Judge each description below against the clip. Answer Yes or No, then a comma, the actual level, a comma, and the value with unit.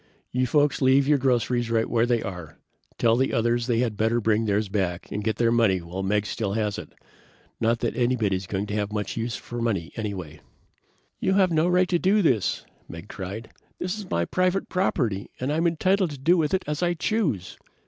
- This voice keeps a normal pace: No, fast, 210 wpm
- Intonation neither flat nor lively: No, wide, 6.4 semitones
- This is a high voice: No, low, 115 Hz